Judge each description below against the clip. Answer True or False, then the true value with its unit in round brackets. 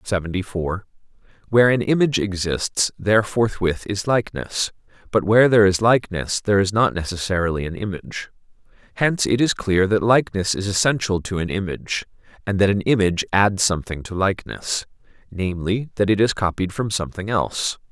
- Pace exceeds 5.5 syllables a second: True (5.9 syllables/s)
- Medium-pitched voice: False (100 Hz)